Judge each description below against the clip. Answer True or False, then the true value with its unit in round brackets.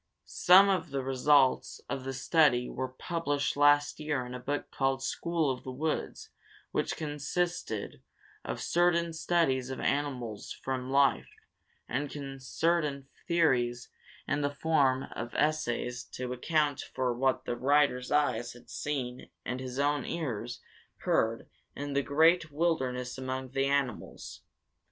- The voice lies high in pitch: False (140 Hz)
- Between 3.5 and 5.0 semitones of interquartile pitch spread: False (2.9 semitones)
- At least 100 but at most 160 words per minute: True (135 wpm)